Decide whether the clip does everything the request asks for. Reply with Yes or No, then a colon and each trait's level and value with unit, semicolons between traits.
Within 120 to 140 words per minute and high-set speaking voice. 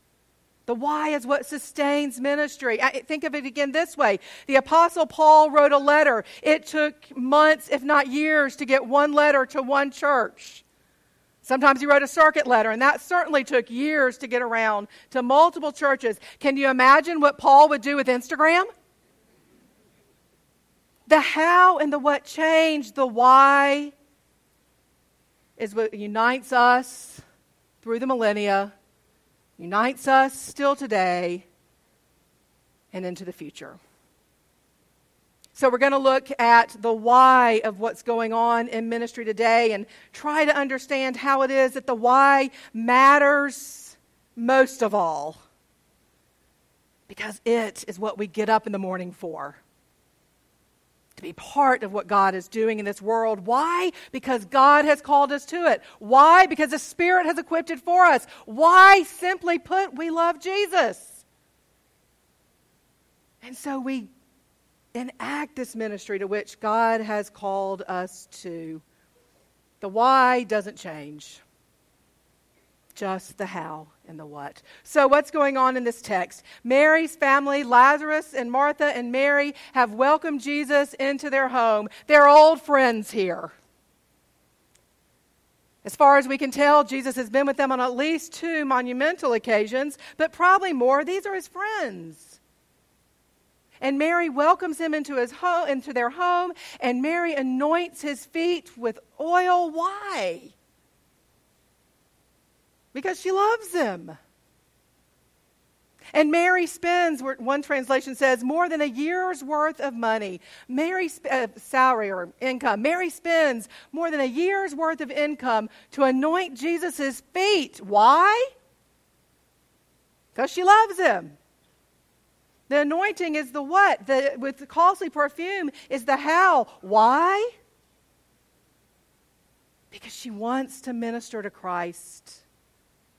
Yes: slow, 135 wpm; very high, 275 Hz